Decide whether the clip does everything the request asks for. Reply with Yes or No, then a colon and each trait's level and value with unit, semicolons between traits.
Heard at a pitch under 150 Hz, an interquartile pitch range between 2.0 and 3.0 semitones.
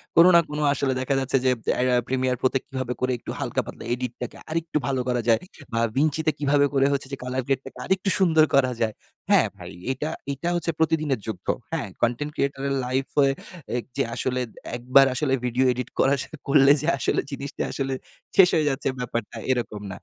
Yes: low, 135 Hz; average, 2.7 semitones